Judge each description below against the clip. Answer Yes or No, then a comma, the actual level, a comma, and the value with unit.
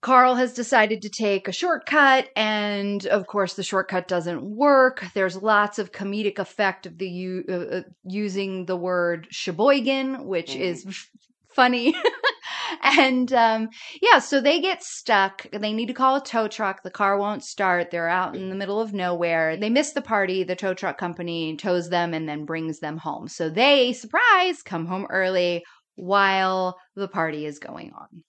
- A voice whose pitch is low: No, high, 200 Hz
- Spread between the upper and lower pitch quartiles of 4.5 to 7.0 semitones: Yes, average, 5.1 semitones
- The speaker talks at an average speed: Yes, average, 175 wpm